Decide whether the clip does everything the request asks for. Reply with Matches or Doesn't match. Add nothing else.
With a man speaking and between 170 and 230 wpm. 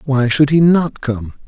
Matches